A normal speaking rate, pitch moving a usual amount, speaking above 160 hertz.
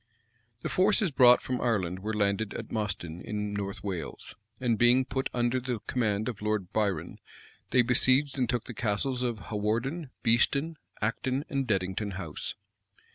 No: average, 155 wpm; average, 3.8 semitones; low, 115 Hz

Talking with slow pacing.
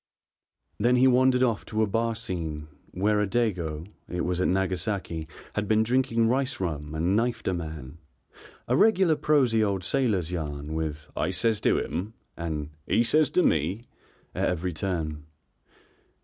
No: average, 160 wpm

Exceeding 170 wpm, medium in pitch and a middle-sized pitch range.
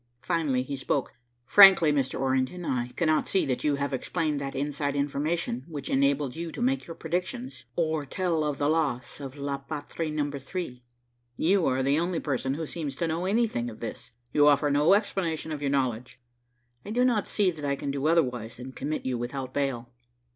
Yes: average, 195 wpm; medium, 145 Hz; average, 3.7 semitones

